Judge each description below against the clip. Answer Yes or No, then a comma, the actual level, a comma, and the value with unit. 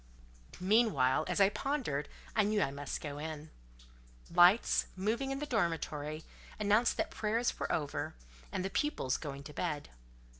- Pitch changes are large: Yes, wide, 6.6 semitones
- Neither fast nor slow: Yes, average, 150 wpm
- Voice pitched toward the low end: No, medium, 180 Hz